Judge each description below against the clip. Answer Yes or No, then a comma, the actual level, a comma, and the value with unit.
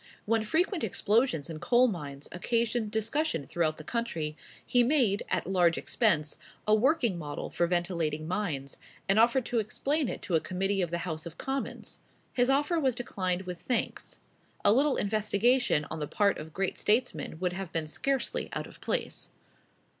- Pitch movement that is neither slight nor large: No, wide, 6.4 semitones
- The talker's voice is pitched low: No, high, 200 Hz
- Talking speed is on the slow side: No, average, 170 wpm